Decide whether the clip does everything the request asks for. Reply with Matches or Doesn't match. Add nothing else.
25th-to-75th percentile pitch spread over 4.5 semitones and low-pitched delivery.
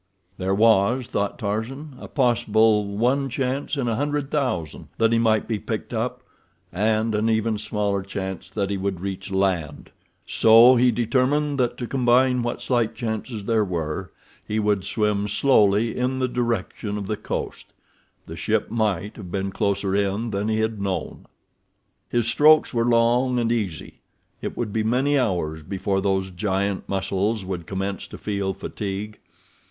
Doesn't match